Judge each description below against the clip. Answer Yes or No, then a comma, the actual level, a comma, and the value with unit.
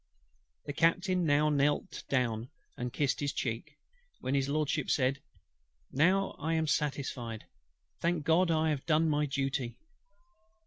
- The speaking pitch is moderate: Yes, medium, 145 Hz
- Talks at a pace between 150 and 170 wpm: No, slow, 135 wpm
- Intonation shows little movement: No, average, 3.1 semitones